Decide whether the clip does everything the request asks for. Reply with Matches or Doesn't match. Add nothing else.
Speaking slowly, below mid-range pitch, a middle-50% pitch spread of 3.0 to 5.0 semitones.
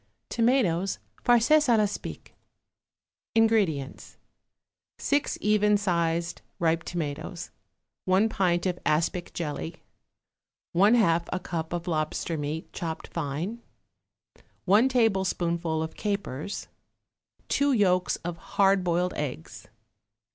Doesn't match